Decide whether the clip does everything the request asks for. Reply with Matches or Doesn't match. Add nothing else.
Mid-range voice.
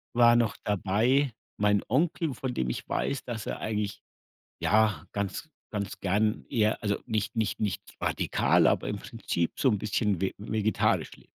Doesn't match